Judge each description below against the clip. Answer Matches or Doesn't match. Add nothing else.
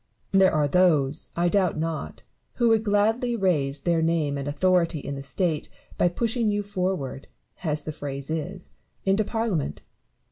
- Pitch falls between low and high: Matches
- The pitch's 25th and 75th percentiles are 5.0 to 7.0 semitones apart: Matches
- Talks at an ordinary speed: Matches